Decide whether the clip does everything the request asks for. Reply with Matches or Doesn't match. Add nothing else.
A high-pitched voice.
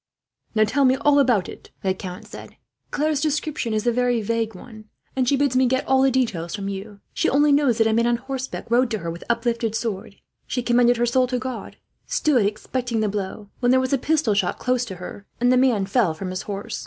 Matches